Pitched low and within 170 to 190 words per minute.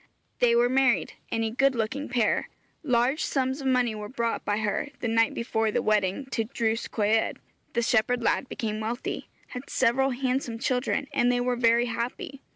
No: high, 240 Hz; average, 175 wpm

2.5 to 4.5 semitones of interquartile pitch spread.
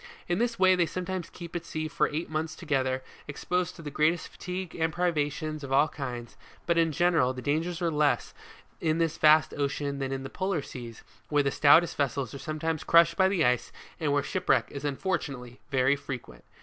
Yes: average, 3.5 semitones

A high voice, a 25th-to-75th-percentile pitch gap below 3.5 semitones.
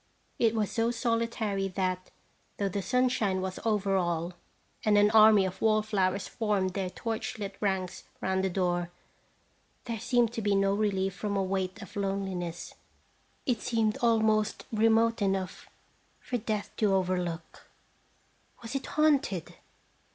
Yes: high, 200 Hz; average, 2.9 semitones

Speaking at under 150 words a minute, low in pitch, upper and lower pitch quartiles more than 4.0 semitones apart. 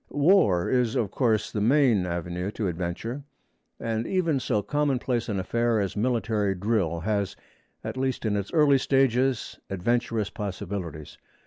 Yes: average, 140 wpm; low, 110 Hz; average, 4.8 semitones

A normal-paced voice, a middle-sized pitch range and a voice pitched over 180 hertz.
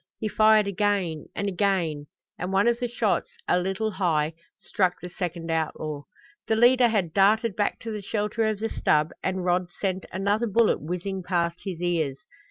Yes: average, 180 wpm; average, 3.7 semitones; high, 190 Hz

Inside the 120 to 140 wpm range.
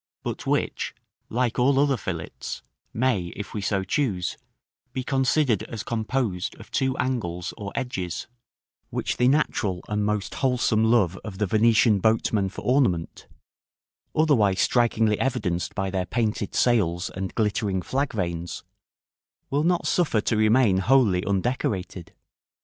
Yes: slow, 135 wpm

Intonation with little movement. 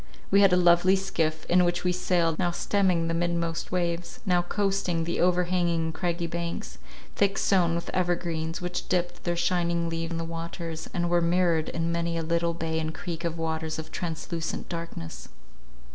Yes: narrow, 1.3 semitones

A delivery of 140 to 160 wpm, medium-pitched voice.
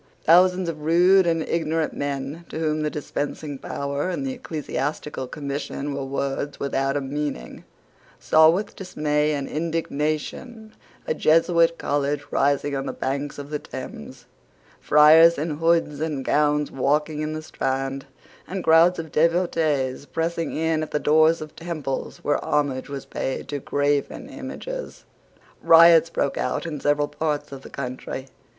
Yes: average, 150 wpm; medium, 150 Hz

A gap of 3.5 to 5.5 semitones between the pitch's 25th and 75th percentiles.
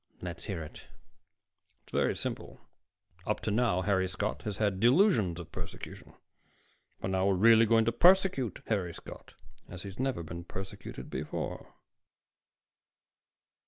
Yes: average, 4.1 semitones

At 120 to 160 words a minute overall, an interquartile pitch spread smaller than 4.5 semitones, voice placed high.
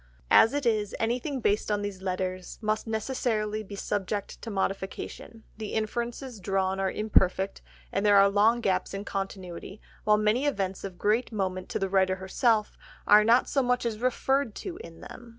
No: average, 175 wpm; average, 3.1 semitones; high, 210 Hz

